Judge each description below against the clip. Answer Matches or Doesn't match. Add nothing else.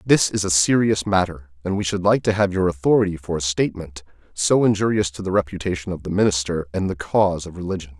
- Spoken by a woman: Doesn't match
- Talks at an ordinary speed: Doesn't match